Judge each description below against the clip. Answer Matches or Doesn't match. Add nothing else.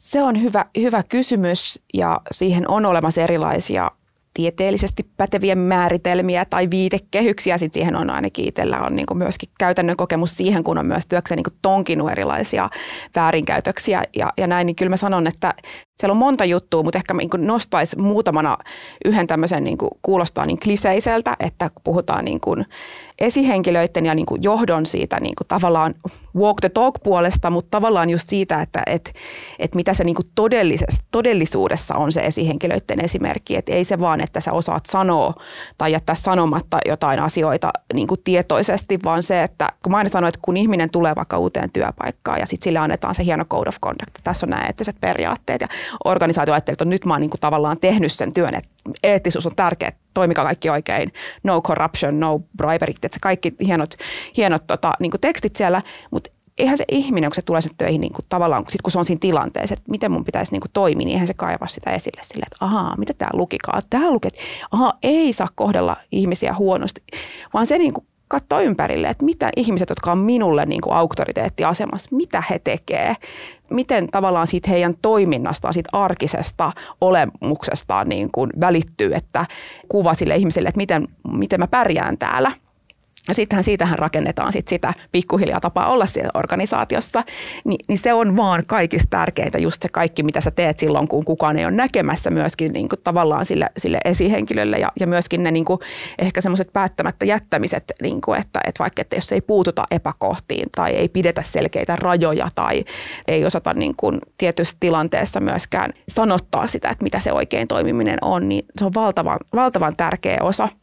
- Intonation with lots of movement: Doesn't match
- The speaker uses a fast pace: Matches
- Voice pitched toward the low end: Doesn't match